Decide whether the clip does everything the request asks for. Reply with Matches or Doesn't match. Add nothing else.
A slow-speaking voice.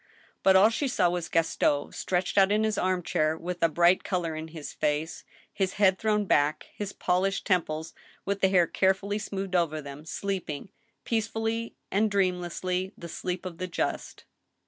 Doesn't match